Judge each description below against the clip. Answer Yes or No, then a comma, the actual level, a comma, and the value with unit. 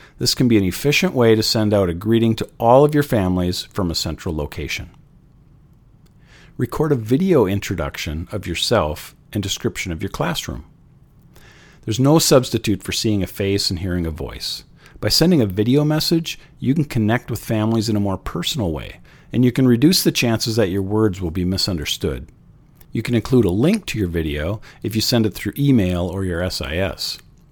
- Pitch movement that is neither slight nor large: No, wide, 6.2 semitones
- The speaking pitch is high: No, low, 110 Hz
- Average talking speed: Yes, average, 190 wpm